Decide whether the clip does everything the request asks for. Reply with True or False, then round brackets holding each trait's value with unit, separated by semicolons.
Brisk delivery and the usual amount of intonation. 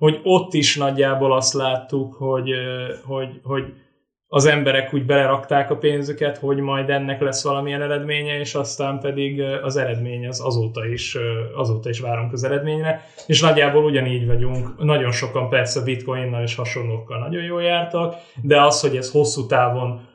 False (160 wpm; 2.3 semitones)